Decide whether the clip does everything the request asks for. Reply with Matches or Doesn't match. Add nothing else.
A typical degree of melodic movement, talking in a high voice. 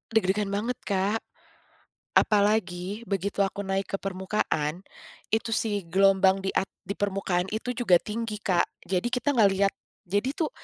Doesn't match